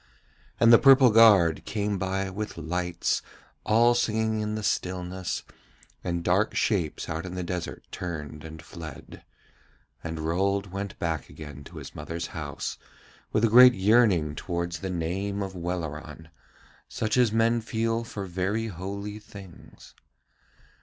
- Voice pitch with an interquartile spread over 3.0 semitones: Yes, average, 4.2 semitones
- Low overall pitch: Yes, very low, 95 Hz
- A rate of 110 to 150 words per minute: Yes, average, 140 wpm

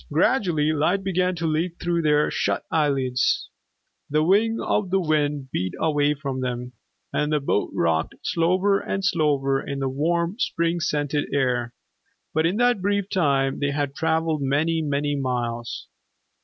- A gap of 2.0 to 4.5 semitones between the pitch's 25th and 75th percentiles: Yes, average, 3.9 semitones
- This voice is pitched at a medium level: Yes, medium, 150 Hz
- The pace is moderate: Yes, average, 150 wpm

